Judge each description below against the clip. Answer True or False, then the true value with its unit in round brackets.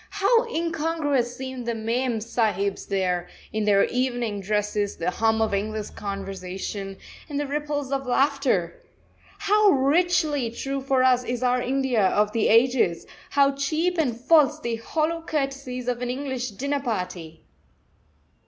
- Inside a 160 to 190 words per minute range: False (145 wpm)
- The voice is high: True (250 Hz)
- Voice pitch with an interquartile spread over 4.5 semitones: True (4.9 semitones)